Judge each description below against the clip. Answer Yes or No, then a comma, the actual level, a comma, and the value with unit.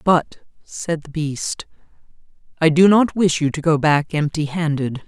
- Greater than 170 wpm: No, average, 165 wpm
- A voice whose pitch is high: No, medium, 160 Hz